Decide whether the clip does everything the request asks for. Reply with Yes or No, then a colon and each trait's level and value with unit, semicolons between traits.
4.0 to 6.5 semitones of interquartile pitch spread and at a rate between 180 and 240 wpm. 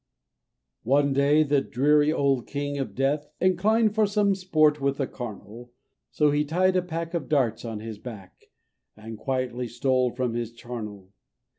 No: average, 4.4 semitones; average, 165 wpm